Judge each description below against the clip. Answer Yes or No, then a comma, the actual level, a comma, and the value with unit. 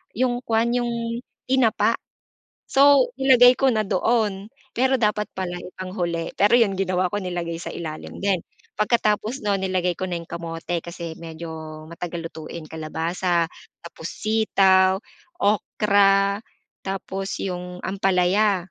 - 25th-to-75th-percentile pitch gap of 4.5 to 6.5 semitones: No, average, 3.9 semitones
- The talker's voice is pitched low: No, high, 190 Hz